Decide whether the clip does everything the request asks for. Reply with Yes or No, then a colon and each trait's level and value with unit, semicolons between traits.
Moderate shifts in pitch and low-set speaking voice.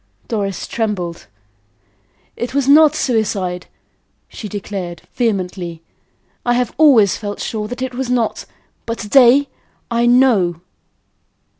No: average, 4.3 semitones; high, 225 Hz